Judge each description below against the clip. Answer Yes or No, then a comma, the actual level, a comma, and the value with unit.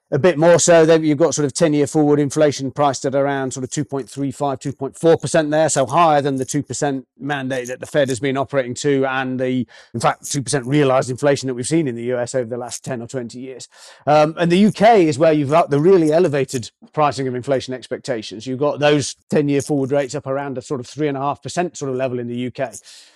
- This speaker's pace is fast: Yes, fast, 225 wpm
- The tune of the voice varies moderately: No, narrow, 2.3 semitones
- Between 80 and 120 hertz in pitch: No, medium, 140 Hz